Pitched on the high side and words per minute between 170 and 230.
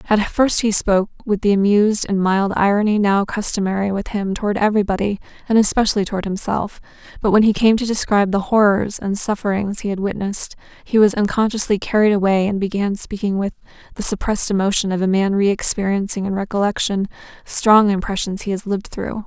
Yes: high, 200 Hz; average, 180 wpm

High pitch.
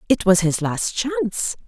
Yes: high, 220 Hz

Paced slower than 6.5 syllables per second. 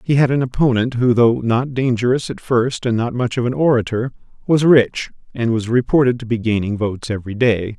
Yes: 5.5 syllables/s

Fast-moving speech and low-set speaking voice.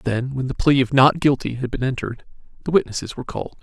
Yes: fast, 230 wpm; low, 130 Hz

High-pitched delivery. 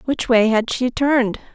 Yes: high, 240 Hz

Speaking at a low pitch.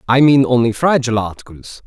Yes: low, 120 Hz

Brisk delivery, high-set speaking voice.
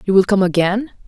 Yes: fast, 225 wpm; high, 200 Hz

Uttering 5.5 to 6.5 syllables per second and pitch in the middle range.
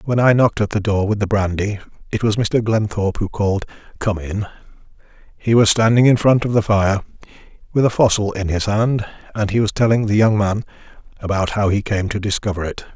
No: 5.7 syllables/s; low, 105 Hz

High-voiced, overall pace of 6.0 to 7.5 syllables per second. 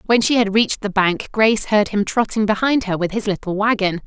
No: high, 210 Hz; 5.7 syllables/s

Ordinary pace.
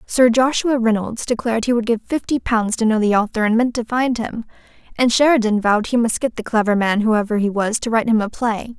No: fast, 240 wpm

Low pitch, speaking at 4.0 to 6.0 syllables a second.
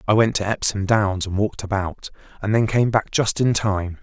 Yes: low, 105 Hz; 5.1 syllables/s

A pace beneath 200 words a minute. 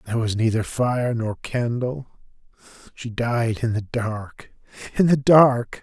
Yes: slow, 135 wpm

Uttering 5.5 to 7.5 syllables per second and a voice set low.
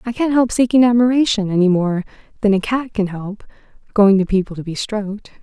No: 5.7 syllables/s; high, 210 Hz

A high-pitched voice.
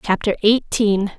Yes: high, 210 Hz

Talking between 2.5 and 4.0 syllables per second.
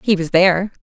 No: 6.1 syllables/s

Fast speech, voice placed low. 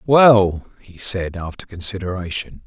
No: slow, 115 wpm; very low, 95 Hz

